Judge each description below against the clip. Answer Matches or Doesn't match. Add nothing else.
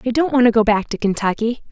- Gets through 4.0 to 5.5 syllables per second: Doesn't match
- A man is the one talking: Doesn't match